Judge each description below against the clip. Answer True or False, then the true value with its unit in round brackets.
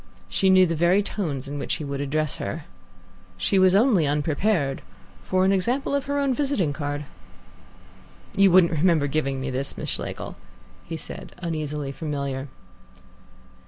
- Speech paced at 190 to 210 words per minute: False (155 wpm)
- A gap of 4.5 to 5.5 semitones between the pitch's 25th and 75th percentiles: True (5.0 semitones)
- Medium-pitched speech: True (160 Hz)